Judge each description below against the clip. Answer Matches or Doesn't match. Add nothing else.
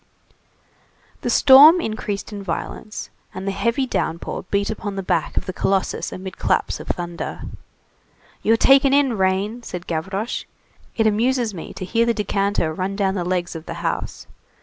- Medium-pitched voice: Doesn't match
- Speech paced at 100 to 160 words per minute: Doesn't match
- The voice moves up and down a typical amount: Matches